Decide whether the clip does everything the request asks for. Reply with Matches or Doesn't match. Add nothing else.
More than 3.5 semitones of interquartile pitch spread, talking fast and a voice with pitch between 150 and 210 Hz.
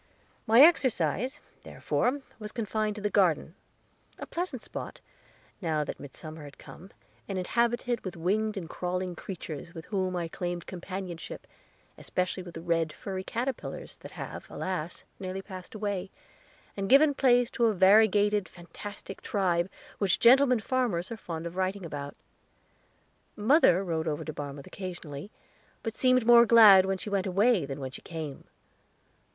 Doesn't match